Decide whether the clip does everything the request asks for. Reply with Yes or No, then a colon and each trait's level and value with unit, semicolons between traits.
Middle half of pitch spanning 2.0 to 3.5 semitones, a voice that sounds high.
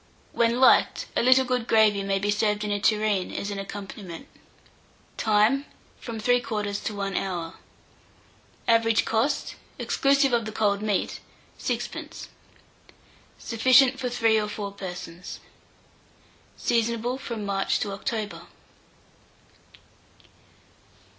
Yes: average, 2.9 semitones; high, 215 Hz